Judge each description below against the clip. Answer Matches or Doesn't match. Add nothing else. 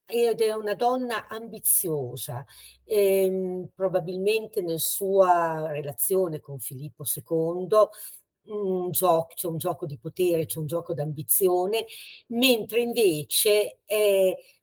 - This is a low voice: Doesn't match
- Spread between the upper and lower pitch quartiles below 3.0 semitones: Doesn't match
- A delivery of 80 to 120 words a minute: Matches